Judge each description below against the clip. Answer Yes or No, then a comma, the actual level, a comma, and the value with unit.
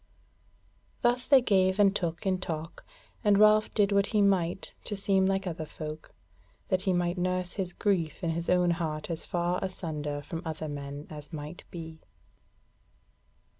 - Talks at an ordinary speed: Yes, average, 165 wpm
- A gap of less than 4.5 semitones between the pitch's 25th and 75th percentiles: Yes, average, 3.4 semitones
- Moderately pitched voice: Yes, medium, 175 Hz